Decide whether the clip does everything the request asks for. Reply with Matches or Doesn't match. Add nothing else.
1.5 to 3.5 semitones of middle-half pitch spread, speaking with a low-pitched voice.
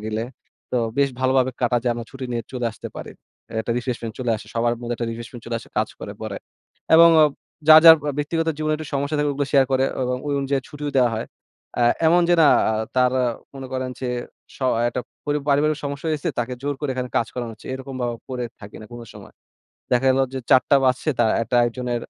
Matches